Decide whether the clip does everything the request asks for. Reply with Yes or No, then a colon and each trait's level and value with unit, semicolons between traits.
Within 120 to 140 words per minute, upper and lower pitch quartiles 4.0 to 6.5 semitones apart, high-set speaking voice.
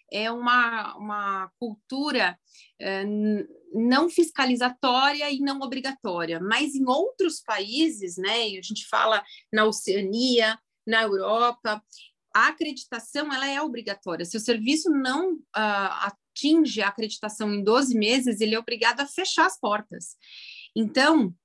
Yes: average, 130 wpm; average, 4.5 semitones; high, 230 Hz